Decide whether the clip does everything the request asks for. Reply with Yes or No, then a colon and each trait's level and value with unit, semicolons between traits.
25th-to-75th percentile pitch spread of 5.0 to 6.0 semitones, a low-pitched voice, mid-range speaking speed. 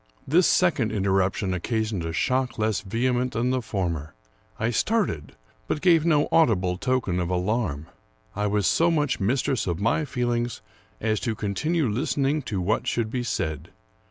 Yes: wide, 5.4 semitones; low, 115 Hz; average, 160 wpm